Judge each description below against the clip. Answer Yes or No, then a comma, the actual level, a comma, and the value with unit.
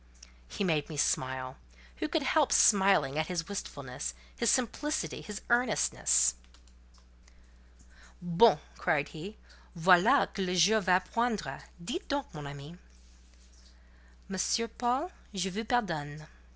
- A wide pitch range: Yes, wide, 7.3 semitones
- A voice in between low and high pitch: Yes, medium, 180 Hz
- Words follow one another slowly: Yes, slow, 125 wpm